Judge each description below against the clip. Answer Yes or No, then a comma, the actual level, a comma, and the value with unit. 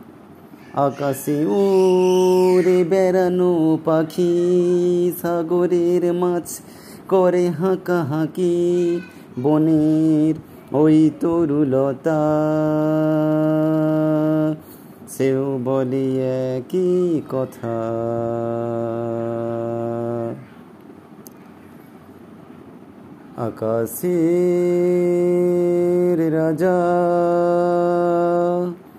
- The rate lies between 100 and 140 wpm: No, average, 35 wpm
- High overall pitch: No, medium, 160 Hz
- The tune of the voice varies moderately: Yes, average, 4.2 semitones